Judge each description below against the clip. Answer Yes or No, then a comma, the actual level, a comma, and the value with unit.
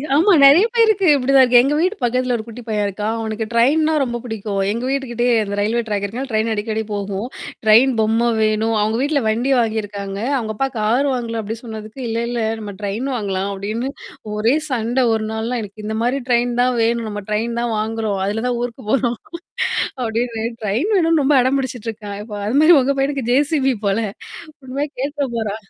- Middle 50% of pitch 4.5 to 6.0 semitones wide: No, average, 3.4 semitones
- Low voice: No, high, 230 Hz